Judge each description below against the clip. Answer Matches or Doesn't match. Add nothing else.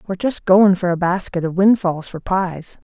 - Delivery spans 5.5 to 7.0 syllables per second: Doesn't match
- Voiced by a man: Doesn't match